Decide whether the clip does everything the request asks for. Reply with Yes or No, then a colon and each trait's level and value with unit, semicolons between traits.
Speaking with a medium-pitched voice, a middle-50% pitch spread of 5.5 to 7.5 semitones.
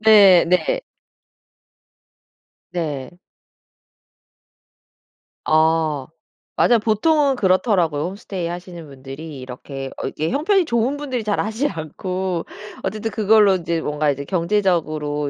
Yes: medium, 180 Hz; wide, 5.8 semitones